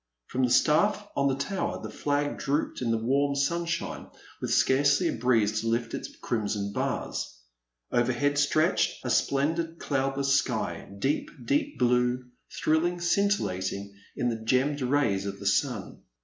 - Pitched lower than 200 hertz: Yes, low, 135 Hz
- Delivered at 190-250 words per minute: No, average, 150 wpm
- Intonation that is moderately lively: Yes, average, 4.1 semitones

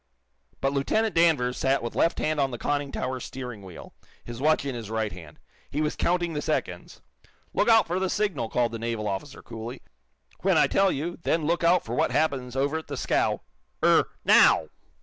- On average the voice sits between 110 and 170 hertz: Yes, low, 135 Hz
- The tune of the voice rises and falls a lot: Yes, wide, 5.7 semitones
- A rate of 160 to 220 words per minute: Yes, average, 200 wpm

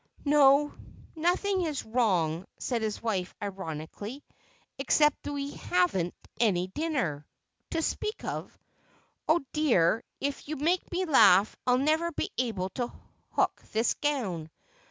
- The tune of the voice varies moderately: No, wide, 8.0 semitones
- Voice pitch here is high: Yes, very high, 250 Hz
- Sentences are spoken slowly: Yes, slow, 125 wpm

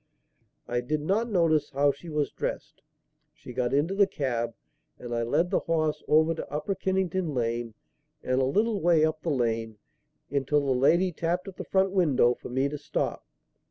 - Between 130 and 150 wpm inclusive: No, average, 185 wpm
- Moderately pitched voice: Yes, medium, 150 Hz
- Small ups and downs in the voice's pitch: No, average, 5.3 semitones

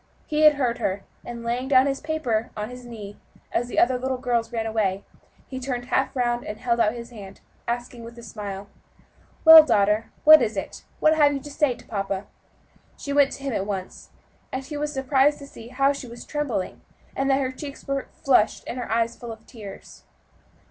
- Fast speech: Yes, fast, 210 wpm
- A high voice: Yes, high, 245 Hz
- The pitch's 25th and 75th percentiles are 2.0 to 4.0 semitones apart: Yes, average, 3.6 semitones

